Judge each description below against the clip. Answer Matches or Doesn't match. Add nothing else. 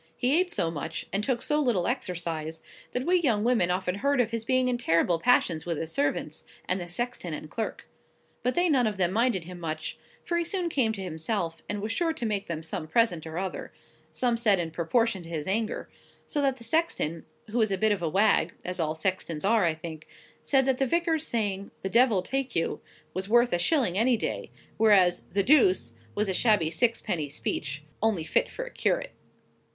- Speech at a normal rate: Doesn't match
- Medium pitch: Doesn't match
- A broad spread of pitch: Matches